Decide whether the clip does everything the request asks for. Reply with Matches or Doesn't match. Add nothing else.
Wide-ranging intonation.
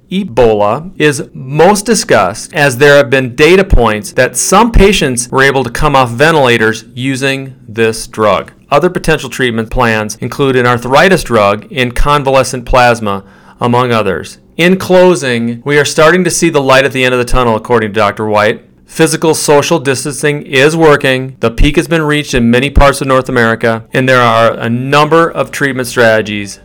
Doesn't match